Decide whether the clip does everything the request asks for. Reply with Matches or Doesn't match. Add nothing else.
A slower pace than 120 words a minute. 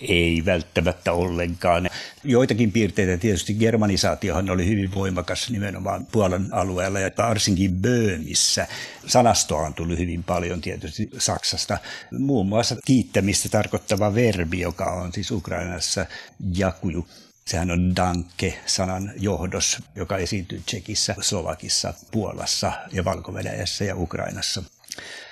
Matches